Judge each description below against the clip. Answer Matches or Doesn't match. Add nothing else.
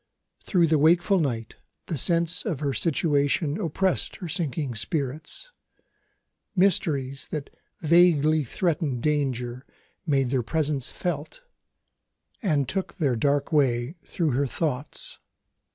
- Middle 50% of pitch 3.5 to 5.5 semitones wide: Matches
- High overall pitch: Doesn't match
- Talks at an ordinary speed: Doesn't match